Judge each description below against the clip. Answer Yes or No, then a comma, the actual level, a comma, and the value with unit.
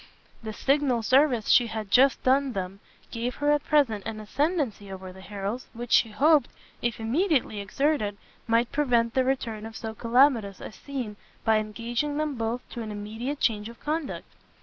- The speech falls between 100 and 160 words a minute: No, average, 170 wpm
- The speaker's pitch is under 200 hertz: No, high, 235 Hz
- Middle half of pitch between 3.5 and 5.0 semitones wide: Yes, average, 4.4 semitones